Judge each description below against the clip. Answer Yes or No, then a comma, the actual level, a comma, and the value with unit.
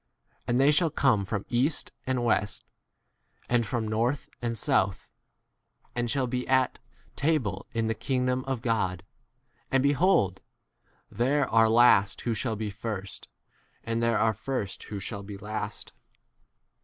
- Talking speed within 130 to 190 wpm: Yes, average, 150 wpm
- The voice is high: No, low, 115 Hz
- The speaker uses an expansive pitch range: No, average, 3.7 semitones